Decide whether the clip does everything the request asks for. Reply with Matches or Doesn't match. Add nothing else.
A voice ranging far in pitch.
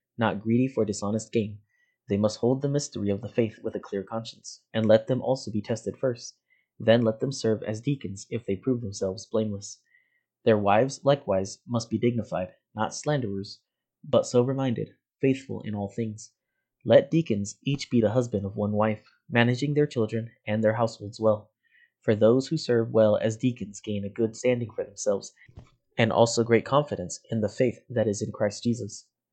Doesn't match